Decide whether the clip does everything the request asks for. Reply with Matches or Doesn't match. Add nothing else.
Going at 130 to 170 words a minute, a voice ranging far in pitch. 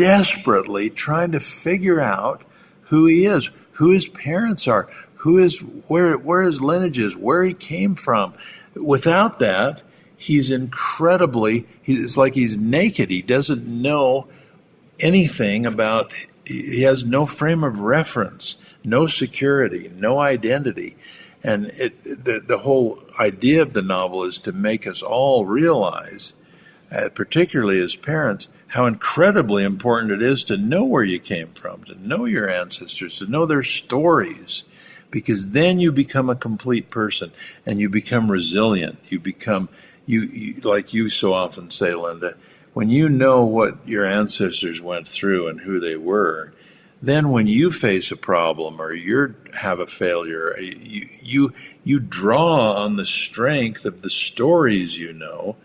Matches